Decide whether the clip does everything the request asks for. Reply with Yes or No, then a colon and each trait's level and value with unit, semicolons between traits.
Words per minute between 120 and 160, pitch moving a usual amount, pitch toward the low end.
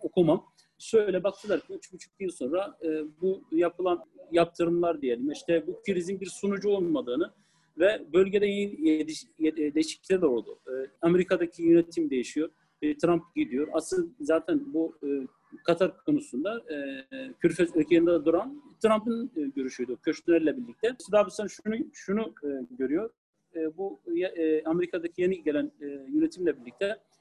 No: fast, 140 wpm; average, 4.4 semitones; medium, 170 Hz